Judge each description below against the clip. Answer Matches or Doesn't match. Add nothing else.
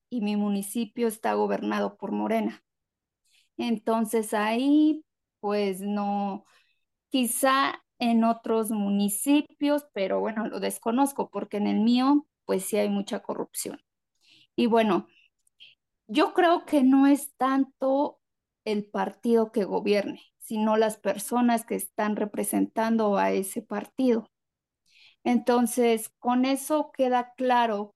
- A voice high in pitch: Matches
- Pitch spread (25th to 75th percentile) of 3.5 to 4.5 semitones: Matches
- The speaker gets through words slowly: Matches